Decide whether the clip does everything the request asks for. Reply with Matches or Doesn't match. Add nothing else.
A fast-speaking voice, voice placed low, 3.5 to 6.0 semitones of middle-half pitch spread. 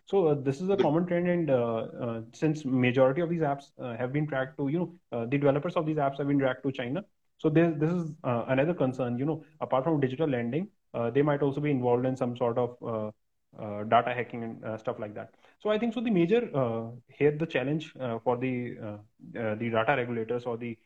Matches